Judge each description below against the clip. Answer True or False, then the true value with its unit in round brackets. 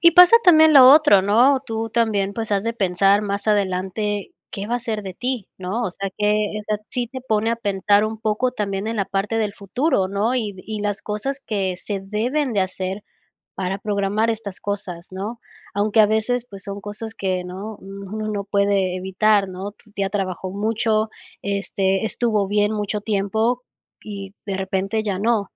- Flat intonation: True (2.2 semitones)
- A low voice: False (205 Hz)